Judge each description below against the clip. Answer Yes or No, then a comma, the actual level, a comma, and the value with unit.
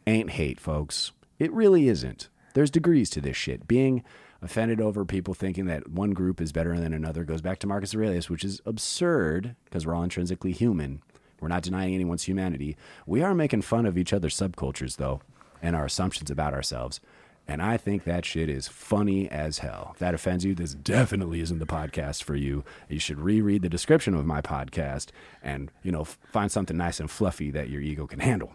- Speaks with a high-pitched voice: No, very low, 90 Hz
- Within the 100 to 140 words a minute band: No, fast, 205 wpm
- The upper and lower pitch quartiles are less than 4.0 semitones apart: No, average, 4.9 semitones